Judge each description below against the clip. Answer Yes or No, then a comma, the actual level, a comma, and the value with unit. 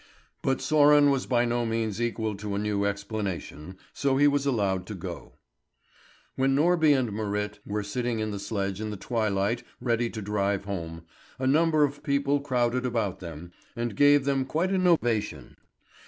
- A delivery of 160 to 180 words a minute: Yes, average, 170 wpm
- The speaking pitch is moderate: No, low, 115 Hz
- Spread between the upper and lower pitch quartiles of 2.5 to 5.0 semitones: No, wide, 5.4 semitones